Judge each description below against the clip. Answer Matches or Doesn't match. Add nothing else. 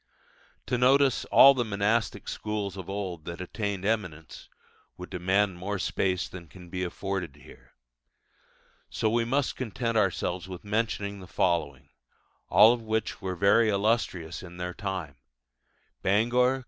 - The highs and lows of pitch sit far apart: Doesn't match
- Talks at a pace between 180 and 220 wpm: Doesn't match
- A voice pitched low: Matches